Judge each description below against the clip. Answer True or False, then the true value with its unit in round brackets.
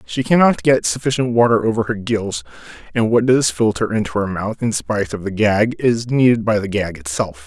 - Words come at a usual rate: False (210 wpm)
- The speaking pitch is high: False (110 Hz)